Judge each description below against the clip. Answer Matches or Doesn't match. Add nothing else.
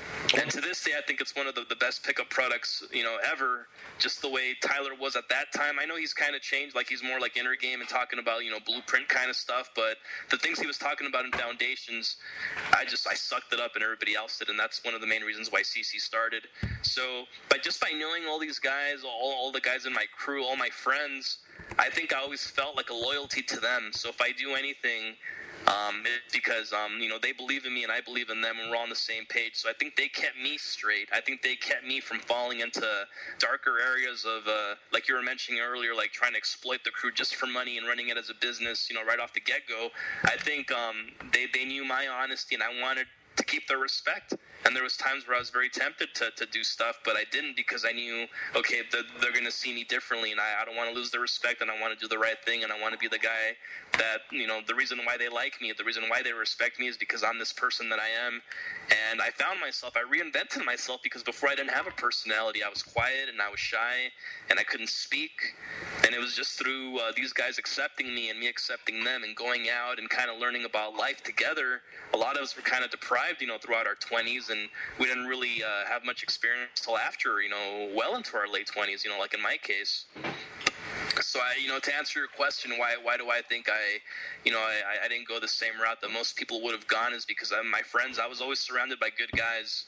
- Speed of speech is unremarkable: Doesn't match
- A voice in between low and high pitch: Doesn't match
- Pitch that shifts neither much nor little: Doesn't match